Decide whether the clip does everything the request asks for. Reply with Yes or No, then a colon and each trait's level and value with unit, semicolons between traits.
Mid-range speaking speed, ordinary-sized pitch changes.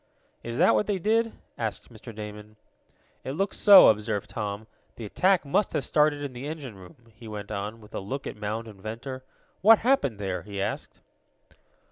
No: average, 185 wpm; wide, 6.1 semitones